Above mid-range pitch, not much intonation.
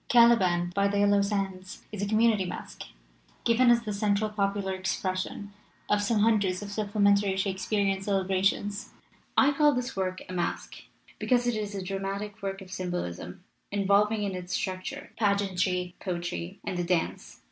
Yes: high, 200 Hz; narrow, 1.9 semitones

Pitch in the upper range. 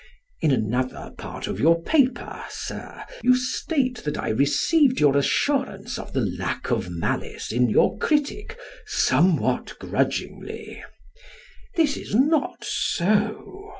Yes: high, 205 Hz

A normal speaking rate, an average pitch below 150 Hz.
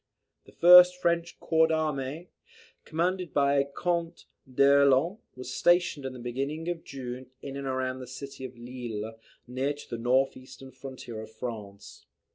Yes: average, 150 wpm; low, 135 Hz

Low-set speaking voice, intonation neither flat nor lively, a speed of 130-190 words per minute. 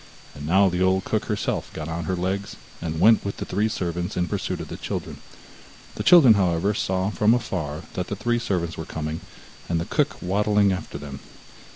No: very low, 95 Hz; average, 3.5 semitones; average, 200 wpm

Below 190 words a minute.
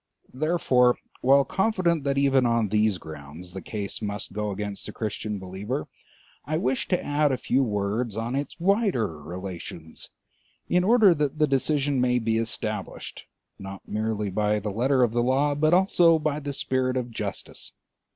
Yes: average, 165 wpm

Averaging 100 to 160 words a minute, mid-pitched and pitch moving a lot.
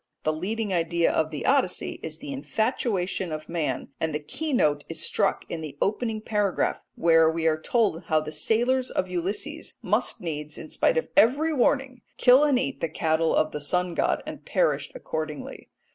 No: average, 185 wpm; medium, 180 Hz; wide, 7.8 semitones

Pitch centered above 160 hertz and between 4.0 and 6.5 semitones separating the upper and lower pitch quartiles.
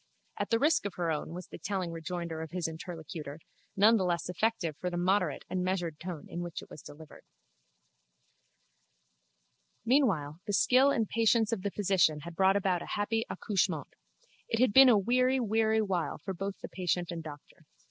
Yes: medium, 185 Hz; average, 4.5 semitones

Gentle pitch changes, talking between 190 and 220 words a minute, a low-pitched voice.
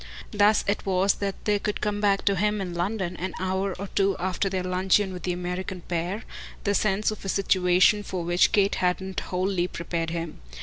No: narrow, 2.0 semitones; average, 200 wpm; high, 190 Hz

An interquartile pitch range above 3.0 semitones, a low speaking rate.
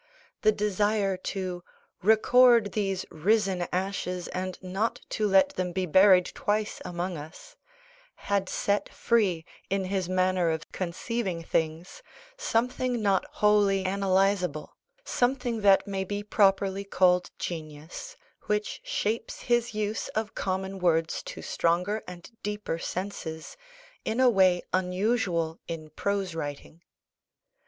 No: average, 2.7 semitones; slow, 120 wpm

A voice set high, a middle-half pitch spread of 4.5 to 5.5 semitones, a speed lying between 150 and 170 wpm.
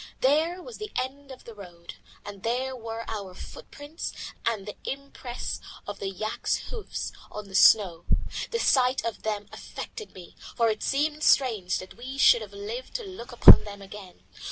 No: high, 230 Hz; average, 5.2 semitones; average, 180 wpm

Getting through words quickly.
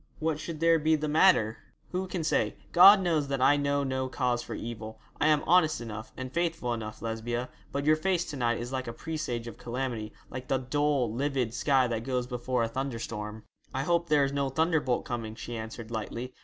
Yes: fast, 210 wpm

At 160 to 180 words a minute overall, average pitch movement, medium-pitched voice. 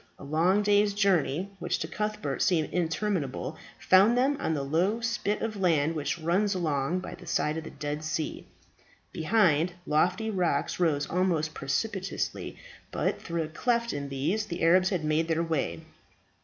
Yes: average, 165 wpm; average, 4.6 semitones; medium, 170 Hz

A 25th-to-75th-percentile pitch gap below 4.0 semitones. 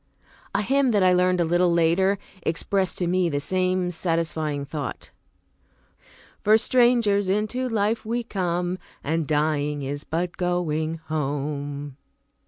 No: average, 4.4 semitones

